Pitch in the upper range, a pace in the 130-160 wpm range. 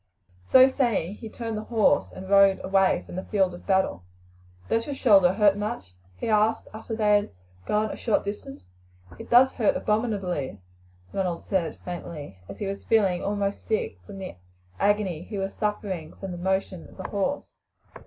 No: high, 200 Hz; average, 175 wpm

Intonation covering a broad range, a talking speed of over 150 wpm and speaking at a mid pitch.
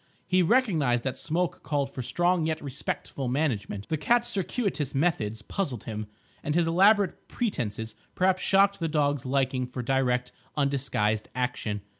No: wide, 6.2 semitones; average, 145 wpm; medium, 145 Hz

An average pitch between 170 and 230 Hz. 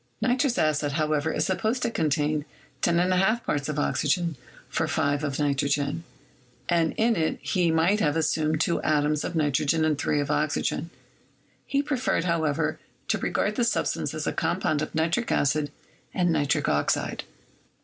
No: medium, 155 Hz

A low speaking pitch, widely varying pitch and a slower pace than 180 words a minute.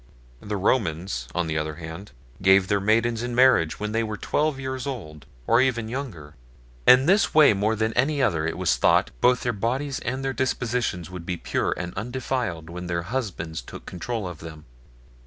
No: low, 110 Hz; wide, 6.8 semitones; average, 190 wpm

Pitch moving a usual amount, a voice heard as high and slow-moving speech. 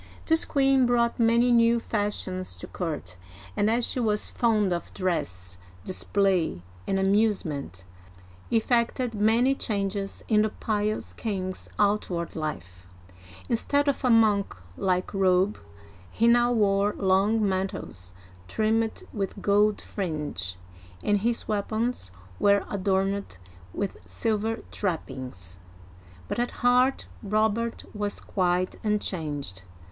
Yes: average, 3.6 semitones; high, 205 Hz; slow, 115 wpm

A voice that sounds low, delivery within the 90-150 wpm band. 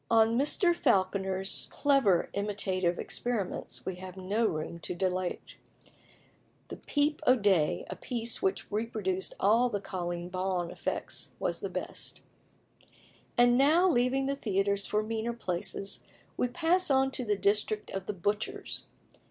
No: high, 210 Hz; average, 140 wpm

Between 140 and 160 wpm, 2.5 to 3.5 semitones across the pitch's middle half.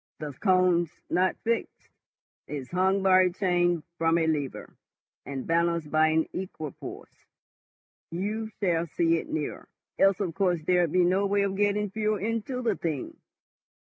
Yes: average, 150 wpm; average, 3.2 semitones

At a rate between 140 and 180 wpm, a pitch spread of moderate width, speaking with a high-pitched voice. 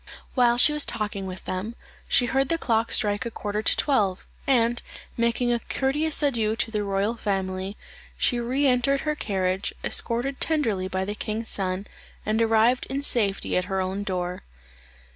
Yes: average, 170 wpm; average, 4.3 semitones; high, 225 Hz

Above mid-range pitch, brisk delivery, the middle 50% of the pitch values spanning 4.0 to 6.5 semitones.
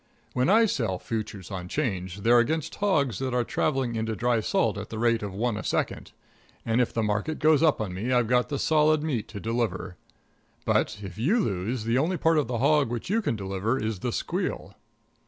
No: low, 120 Hz; fast, 210 wpm; average, 5.1 semitones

